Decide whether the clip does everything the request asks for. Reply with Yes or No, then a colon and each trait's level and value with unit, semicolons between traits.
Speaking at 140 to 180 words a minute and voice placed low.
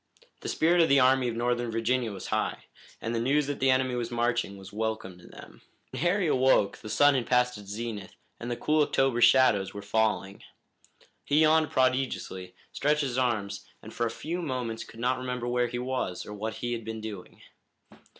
No: average, 200 wpm; low, 120 Hz